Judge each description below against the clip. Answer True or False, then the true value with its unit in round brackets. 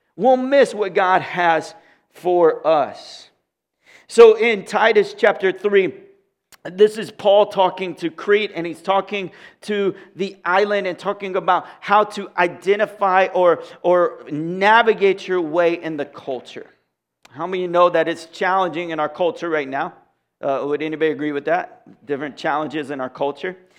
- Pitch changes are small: False (3.8 semitones)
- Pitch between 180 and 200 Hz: True (185 Hz)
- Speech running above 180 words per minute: False (155 wpm)